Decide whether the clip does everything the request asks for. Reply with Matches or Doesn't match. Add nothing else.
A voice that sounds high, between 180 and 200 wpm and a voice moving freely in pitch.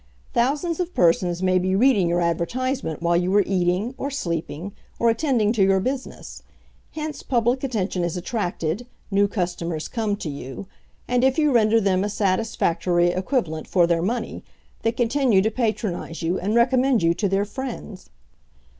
Doesn't match